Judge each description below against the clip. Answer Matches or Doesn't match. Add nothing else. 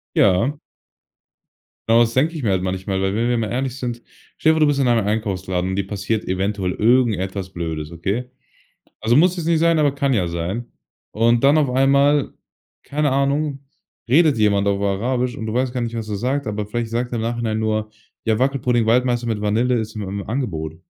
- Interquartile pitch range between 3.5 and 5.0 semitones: Matches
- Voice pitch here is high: Doesn't match